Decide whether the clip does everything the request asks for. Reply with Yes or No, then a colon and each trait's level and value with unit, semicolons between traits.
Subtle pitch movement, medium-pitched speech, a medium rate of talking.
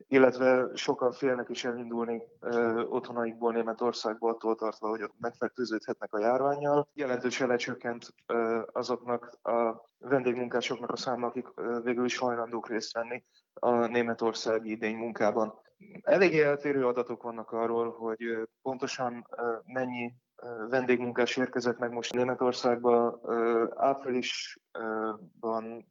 No: narrow, 1.4 semitones; low, 120 Hz; average, 120 wpm